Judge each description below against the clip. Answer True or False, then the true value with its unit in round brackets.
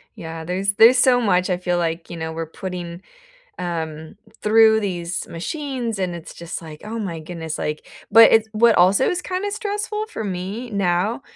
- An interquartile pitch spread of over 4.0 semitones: True (5.1 semitones)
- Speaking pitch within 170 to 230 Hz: True (185 Hz)